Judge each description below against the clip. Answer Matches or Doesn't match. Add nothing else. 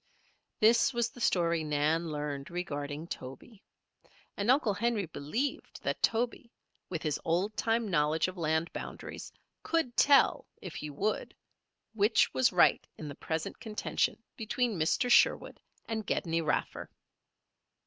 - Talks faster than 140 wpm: Doesn't match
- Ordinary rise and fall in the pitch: Doesn't match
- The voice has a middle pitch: Matches